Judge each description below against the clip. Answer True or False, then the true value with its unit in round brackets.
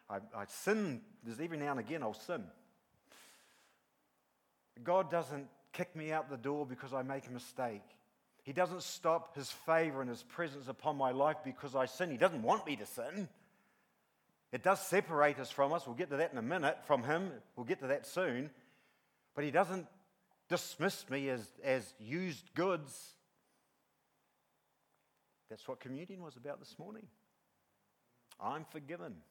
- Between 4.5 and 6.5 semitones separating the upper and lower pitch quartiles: True (5.0 semitones)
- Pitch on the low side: False (155 Hz)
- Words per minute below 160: False (165 wpm)